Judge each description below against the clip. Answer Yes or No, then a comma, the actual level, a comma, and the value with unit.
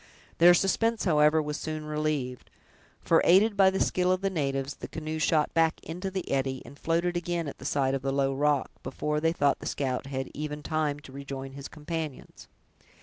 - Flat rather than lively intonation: No, average, 3.4 semitones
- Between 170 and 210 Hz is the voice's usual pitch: No, medium, 150 Hz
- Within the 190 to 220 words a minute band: Yes, average, 200 wpm